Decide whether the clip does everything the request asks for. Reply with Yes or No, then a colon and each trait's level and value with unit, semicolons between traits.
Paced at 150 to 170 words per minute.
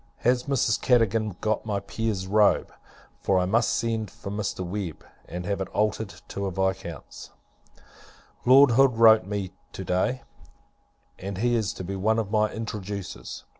Yes: average, 165 wpm